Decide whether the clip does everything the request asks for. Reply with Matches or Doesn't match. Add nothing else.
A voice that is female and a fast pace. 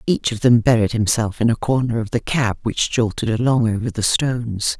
Matches